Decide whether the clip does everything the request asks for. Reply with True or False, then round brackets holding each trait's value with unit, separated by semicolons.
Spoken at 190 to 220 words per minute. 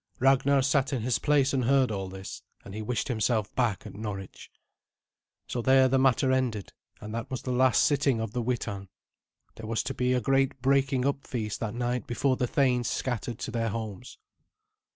True (195 wpm)